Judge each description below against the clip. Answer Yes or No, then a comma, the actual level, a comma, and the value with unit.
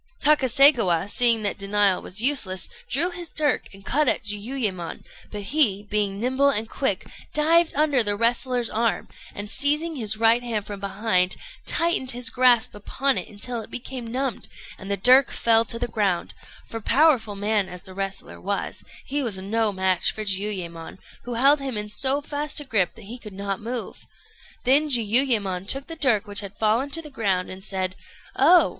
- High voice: Yes, high, 225 Hz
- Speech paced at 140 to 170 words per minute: No, average, 180 wpm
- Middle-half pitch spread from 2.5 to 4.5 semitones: No, average, 5.0 semitones